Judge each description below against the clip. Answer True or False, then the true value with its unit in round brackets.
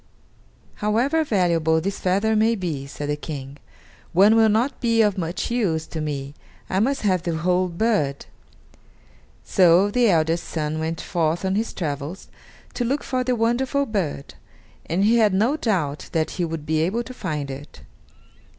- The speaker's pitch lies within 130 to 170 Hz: False (185 Hz)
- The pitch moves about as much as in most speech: False (5.9 semitones)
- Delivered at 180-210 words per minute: False (170 wpm)